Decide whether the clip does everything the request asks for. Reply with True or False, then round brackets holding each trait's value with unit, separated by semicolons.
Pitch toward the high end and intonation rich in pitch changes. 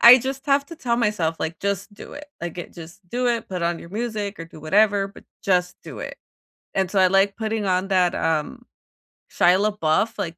False (195 Hz; 4.2 semitones)